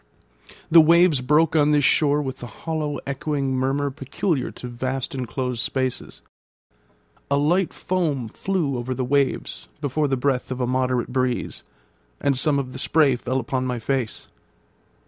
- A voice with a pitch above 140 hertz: No, low, 135 Hz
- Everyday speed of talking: Yes, average, 155 wpm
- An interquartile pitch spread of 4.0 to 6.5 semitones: No, narrow, 2.6 semitones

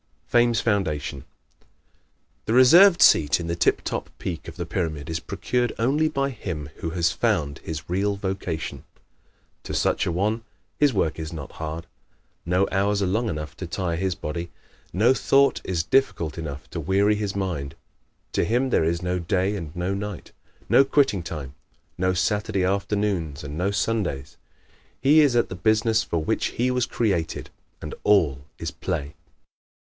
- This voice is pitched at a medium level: No, very low, 95 Hz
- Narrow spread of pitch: No, average, 5.0 semitones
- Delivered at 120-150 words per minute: No, average, 170 wpm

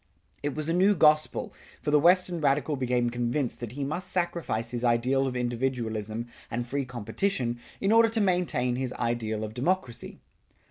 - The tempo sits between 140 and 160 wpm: No, average, 170 wpm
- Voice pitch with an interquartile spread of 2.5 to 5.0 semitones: No, wide, 5.6 semitones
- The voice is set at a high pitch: No, low, 130 Hz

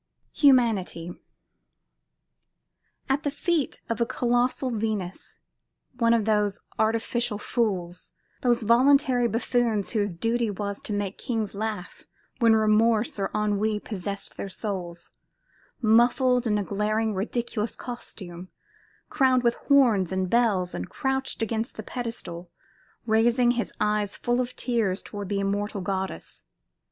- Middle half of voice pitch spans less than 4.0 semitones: Yes, average, 3.1 semitones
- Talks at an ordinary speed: No, slow, 125 wpm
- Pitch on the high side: Yes, high, 220 Hz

